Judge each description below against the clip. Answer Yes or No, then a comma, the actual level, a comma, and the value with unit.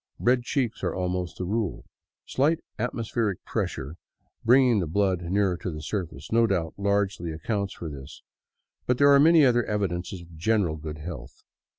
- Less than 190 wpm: Yes, average, 160 wpm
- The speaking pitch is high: No, low, 100 Hz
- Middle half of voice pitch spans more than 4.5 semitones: Yes, wide, 5.6 semitones